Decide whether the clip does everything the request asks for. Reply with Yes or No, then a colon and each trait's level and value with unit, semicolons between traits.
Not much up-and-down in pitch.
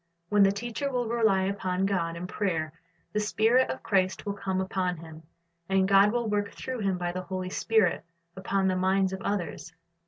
Yes: narrow, 2.2 semitones